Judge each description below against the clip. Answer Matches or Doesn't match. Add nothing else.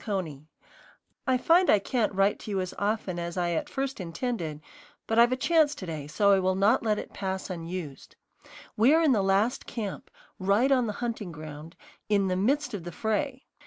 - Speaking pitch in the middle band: Doesn't match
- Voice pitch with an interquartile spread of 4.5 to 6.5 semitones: Matches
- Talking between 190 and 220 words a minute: Matches